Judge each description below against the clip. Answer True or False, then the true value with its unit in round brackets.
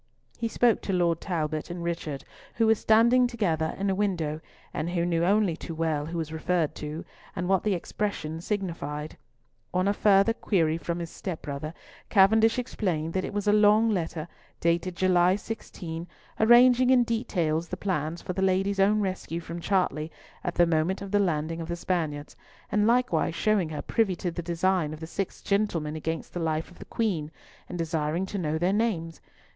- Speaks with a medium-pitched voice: True (175 Hz)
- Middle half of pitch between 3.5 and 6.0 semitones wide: True (3.9 semitones)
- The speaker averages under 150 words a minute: False (190 wpm)